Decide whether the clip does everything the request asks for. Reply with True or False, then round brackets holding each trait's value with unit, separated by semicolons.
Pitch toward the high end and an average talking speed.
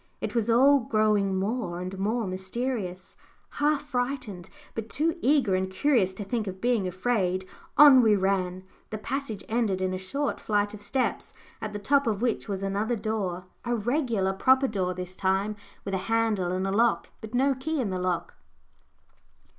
True (210 Hz; 180 wpm)